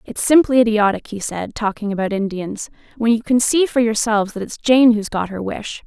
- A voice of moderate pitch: No, high, 225 Hz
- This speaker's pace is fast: Yes, fast, 215 wpm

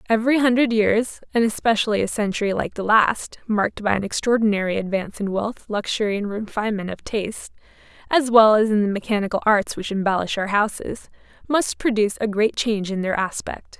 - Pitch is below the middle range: No, high, 215 Hz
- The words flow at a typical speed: Yes, average, 180 wpm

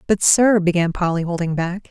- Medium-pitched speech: Yes, medium, 180 Hz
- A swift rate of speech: No, average, 190 wpm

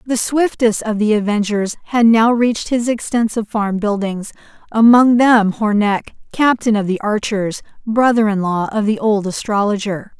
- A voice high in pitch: Yes, high, 215 Hz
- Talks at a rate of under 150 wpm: No, average, 155 wpm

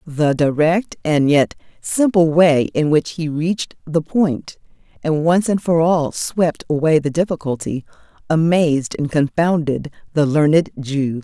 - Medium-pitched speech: Yes, medium, 155 Hz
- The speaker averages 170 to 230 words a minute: No, average, 145 wpm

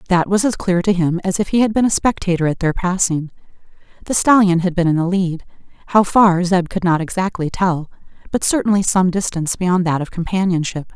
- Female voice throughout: Yes, female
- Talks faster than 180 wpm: Yes, fast, 205 wpm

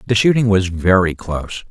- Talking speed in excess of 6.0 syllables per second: No, 5.4 syllables/s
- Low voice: Yes, low, 100 Hz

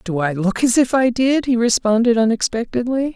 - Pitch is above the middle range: Yes, high, 235 Hz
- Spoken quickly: No, average, 190 wpm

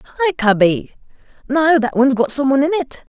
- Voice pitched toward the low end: No, very high, 275 Hz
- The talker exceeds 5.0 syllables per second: Yes, 6.5 syllables/s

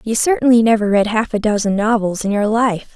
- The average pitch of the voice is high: Yes, high, 220 Hz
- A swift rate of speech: Yes, fast, 225 wpm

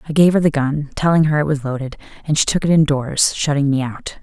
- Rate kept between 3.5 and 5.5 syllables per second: No, 5.9 syllables/s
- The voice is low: No, medium, 145 Hz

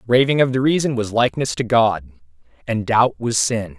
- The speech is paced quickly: No, average, 190 wpm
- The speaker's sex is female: No, male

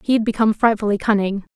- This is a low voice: No, high, 210 Hz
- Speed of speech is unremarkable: Yes, average, 195 wpm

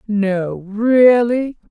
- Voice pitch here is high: Yes, high, 220 Hz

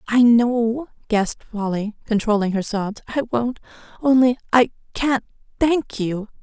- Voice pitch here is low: No, high, 230 Hz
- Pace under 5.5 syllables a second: Yes, 4.2 syllables/s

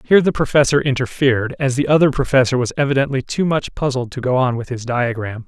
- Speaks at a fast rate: Yes, fast, 210 wpm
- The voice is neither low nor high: No, low, 130 Hz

